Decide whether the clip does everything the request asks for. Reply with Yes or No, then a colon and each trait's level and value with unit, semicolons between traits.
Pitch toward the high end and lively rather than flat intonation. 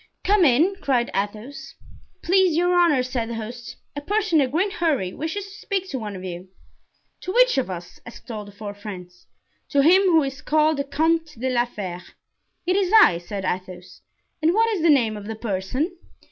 Yes: very high, 270 Hz; wide, 8.7 semitones